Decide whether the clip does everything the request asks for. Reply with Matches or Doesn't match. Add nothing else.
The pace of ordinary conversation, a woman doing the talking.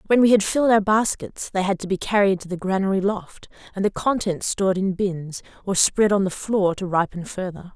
Doesn't match